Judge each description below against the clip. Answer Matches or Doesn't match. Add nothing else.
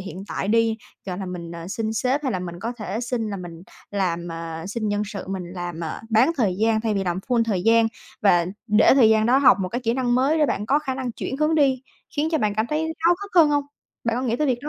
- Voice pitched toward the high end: Matches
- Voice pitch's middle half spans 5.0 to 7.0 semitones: Matches